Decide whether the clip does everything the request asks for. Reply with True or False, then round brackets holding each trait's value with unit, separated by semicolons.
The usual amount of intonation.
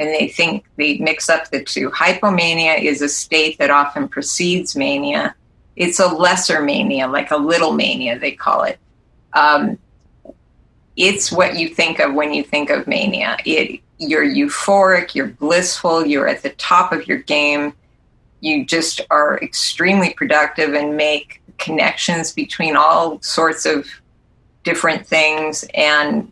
False (8.9 semitones)